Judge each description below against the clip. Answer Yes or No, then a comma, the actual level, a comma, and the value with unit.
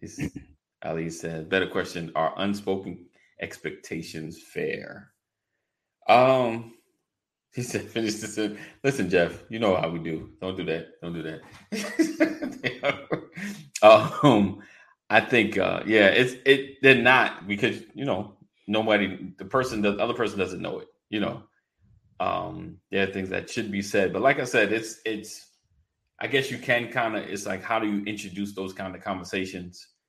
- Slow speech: No, average, 160 wpm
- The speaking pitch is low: Yes, low, 105 Hz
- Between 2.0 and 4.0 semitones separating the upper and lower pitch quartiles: No, average, 5.0 semitones